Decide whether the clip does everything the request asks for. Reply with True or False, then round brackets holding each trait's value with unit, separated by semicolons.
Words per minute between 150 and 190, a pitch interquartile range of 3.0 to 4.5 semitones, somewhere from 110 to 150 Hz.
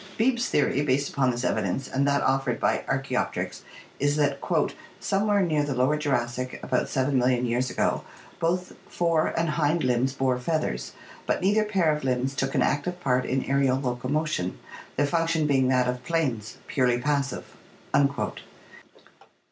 True (155 wpm; 3.6 semitones; 140 Hz)